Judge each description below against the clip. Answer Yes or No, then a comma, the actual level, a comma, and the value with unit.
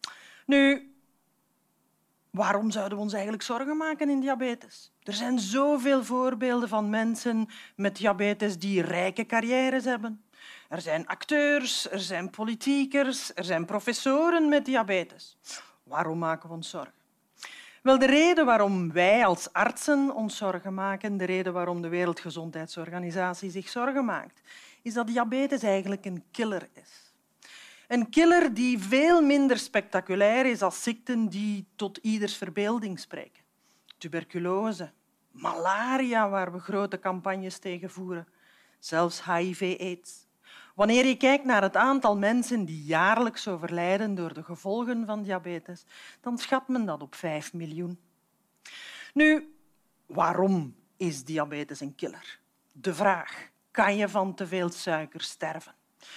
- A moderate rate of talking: No, slow, 130 wpm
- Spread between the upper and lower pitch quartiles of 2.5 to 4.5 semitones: No, wide, 5.6 semitones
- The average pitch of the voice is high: Yes, high, 205 Hz